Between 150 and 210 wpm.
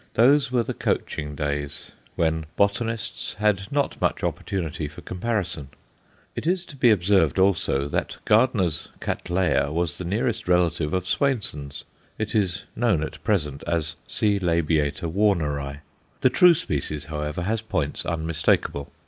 No: average, 140 wpm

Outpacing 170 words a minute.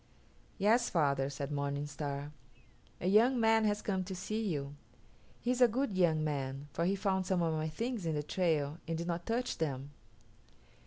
Yes: average, 190 wpm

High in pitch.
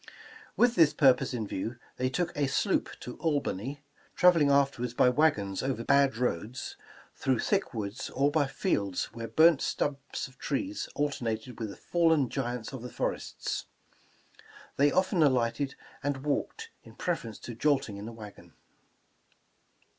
No: low, 135 Hz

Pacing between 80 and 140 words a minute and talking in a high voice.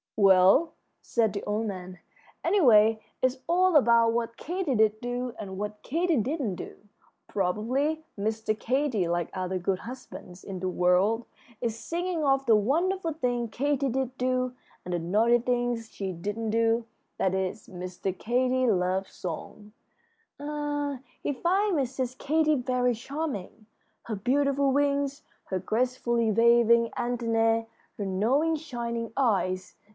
Yes: slow, 135 wpm; high, 235 Hz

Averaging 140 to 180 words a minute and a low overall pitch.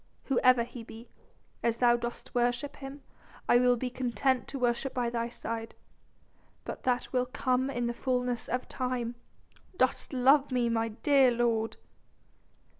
No: average, 150 wpm; high, 245 Hz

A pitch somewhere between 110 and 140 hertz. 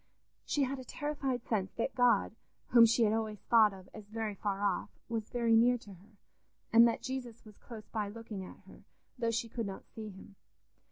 No: high, 225 Hz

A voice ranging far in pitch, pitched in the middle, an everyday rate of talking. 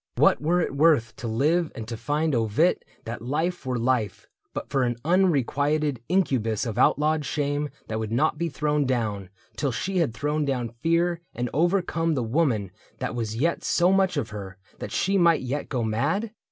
Yes: wide, 6.0 semitones; medium, 145 Hz; average, 185 wpm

